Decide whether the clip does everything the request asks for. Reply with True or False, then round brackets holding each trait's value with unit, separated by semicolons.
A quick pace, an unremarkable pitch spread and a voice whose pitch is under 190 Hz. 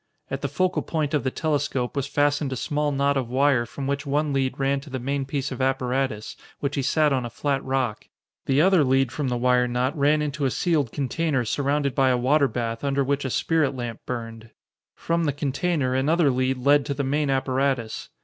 False (215 wpm; 2.1 semitones; 135 Hz)